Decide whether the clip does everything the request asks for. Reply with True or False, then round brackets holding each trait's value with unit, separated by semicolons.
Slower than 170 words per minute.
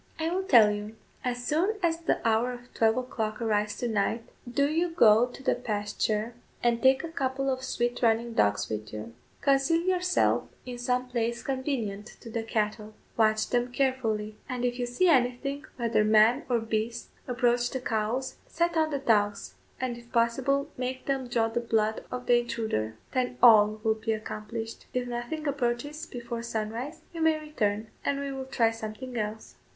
False (180 wpm)